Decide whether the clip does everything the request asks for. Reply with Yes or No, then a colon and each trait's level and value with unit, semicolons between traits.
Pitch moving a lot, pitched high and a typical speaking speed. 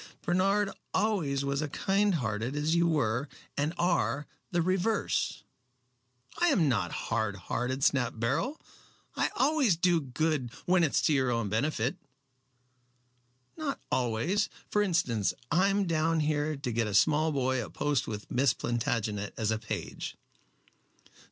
No: wide, 6.8 semitones; medium, 145 Hz; average, 150 wpm